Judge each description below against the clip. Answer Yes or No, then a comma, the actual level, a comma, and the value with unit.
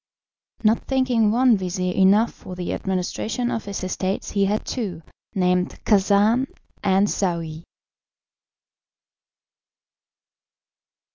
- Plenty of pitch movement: No, average, 3.4 semitones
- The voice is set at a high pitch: Yes, high, 200 Hz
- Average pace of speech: No, slow, 95 wpm